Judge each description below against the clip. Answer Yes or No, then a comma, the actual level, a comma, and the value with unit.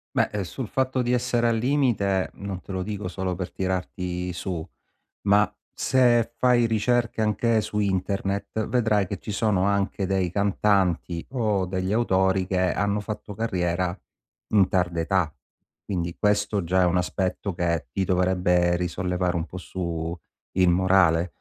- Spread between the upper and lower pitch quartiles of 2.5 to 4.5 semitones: Yes, average, 2.8 semitones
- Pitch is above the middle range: No, very low, 95 Hz